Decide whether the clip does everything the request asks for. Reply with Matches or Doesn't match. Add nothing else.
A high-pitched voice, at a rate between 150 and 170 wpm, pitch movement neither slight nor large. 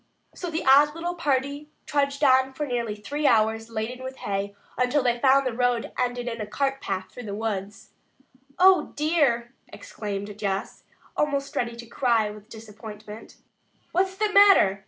Matches